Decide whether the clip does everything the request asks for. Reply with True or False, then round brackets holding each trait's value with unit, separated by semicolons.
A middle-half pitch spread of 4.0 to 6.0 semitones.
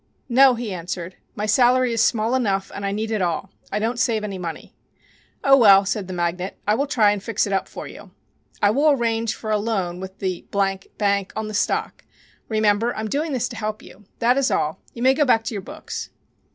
False (3.4 semitones)